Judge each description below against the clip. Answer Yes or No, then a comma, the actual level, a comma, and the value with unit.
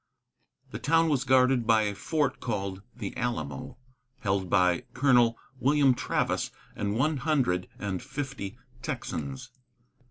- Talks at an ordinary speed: No, slow, 125 wpm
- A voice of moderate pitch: No, low, 120 Hz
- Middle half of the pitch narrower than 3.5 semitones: No, wide, 5.6 semitones